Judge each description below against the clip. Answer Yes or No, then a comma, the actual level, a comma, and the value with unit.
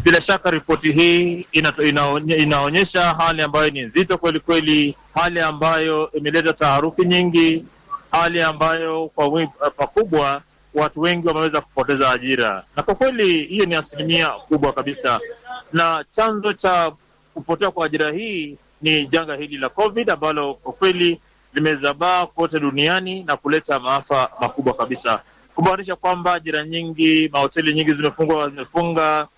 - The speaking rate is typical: Yes, average, 130 wpm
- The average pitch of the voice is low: No, medium, 160 Hz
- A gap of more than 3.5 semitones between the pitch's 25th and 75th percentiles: No, narrow, 2.5 semitones